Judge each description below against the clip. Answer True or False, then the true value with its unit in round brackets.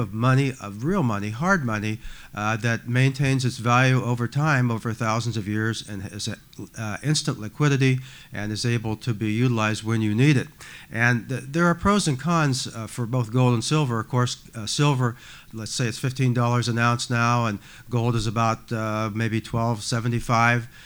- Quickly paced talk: False (185 wpm)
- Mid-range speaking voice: False (120 Hz)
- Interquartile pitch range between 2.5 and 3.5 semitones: True (2.8 semitones)